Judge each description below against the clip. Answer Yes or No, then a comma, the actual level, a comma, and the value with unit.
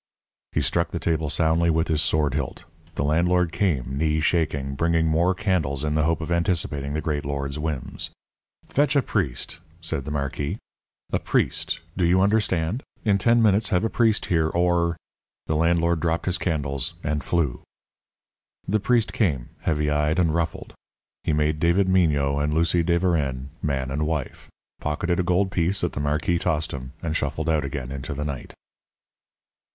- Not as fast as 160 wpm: No, average, 175 wpm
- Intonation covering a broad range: No, average, 3.2 semitones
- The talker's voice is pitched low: Yes, very low, 80 Hz